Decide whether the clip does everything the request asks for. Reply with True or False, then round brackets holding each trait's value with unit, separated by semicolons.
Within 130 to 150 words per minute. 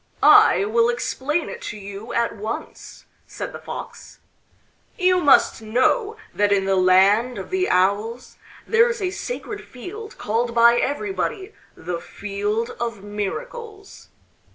True (135 wpm)